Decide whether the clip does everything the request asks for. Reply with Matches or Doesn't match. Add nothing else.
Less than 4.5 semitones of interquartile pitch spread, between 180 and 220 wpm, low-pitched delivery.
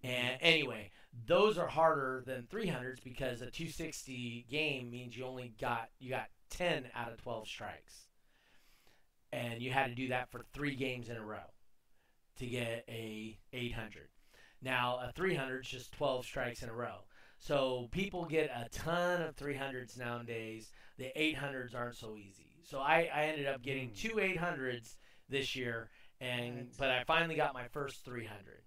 Doesn't match